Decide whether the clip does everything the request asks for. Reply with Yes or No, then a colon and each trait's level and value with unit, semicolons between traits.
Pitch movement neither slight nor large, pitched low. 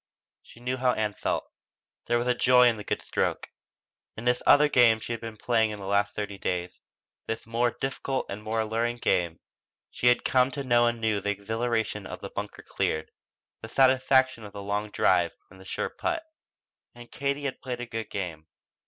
Yes: average, 3.3 semitones; low, 115 Hz